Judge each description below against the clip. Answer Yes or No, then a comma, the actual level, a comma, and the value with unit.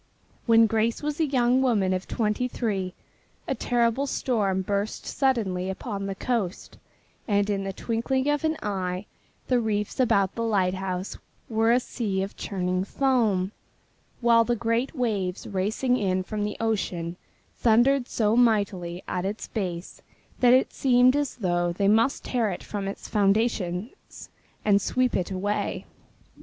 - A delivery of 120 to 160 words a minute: Yes, average, 150 wpm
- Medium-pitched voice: No, high, 215 Hz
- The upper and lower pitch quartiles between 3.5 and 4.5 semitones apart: Yes, average, 4.1 semitones